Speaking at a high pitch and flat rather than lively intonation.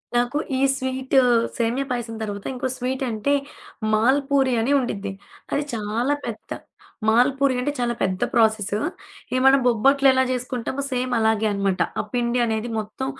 No: high, 245 Hz; average, 3.1 semitones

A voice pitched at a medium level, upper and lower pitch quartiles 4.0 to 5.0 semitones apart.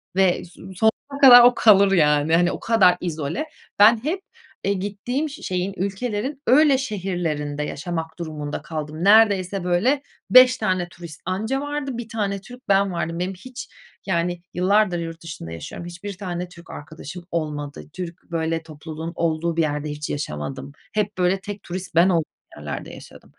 Yes: medium, 180 Hz; average, 4.3 semitones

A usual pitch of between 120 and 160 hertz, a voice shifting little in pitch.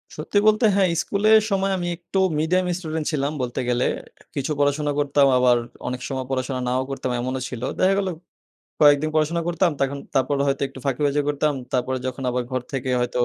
No: medium, 140 Hz; average, 4.6 semitones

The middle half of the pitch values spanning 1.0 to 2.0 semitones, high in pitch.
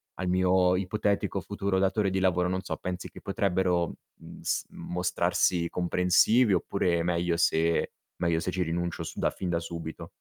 No: narrow, 1.5 semitones; very low, 90 Hz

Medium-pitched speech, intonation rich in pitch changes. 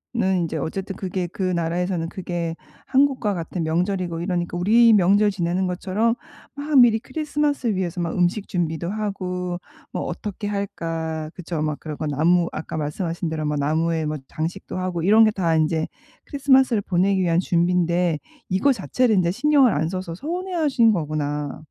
No: medium, 180 Hz; average, 4.1 semitones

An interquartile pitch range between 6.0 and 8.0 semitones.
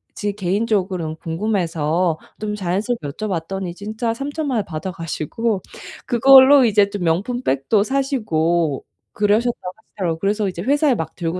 No: average, 5.2 semitones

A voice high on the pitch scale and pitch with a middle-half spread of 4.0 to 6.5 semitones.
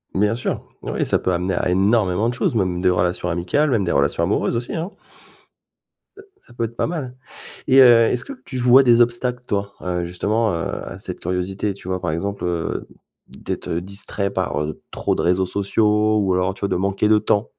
No: low, 100 Hz; average, 4.5 semitones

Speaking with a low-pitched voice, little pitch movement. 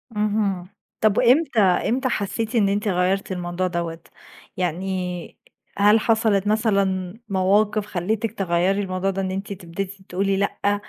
No: high, 195 Hz; narrow, 2.3 semitones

